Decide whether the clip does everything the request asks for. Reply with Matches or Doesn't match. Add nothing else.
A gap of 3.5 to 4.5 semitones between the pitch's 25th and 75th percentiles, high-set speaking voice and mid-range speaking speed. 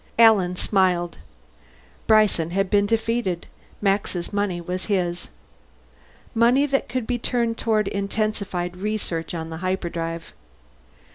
Doesn't match